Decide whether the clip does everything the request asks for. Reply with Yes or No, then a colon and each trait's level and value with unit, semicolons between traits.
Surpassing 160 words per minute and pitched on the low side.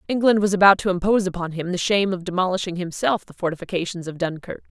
No: average, 200 wpm; medium, 185 Hz